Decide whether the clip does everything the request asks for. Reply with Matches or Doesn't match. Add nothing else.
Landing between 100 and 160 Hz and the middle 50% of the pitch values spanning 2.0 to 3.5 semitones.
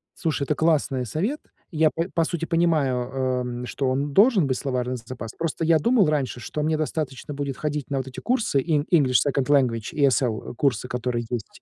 Doesn't match